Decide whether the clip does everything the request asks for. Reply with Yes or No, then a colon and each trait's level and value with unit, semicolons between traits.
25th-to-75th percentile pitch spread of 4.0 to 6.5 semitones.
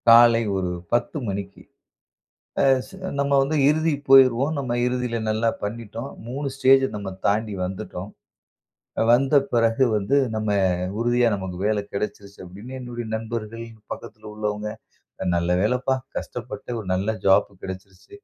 No: average, 3.5 semitones